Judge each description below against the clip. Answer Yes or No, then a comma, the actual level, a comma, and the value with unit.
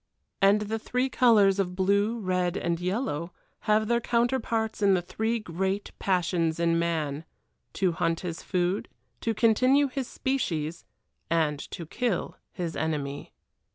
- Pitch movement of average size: Yes, average, 4.8 semitones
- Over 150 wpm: No, average, 140 wpm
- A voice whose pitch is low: No, high, 190 Hz